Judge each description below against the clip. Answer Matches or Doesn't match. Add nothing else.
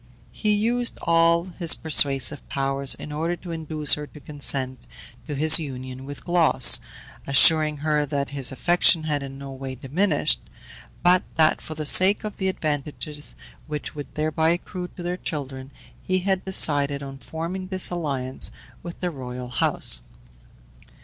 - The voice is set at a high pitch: Doesn't match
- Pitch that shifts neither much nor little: Matches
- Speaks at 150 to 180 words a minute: Matches